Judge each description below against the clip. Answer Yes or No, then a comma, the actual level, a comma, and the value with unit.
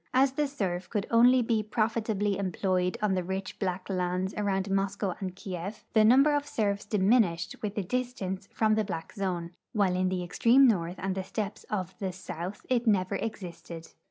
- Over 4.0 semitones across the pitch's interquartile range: No, average, 2.9 semitones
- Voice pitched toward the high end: Yes, high, 195 Hz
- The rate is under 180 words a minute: No, average, 185 wpm